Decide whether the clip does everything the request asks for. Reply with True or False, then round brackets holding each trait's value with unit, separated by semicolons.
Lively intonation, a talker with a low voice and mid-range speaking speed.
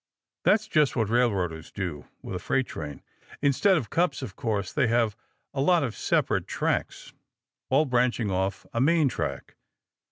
True (6.1 semitones; 120 Hz; 160 wpm)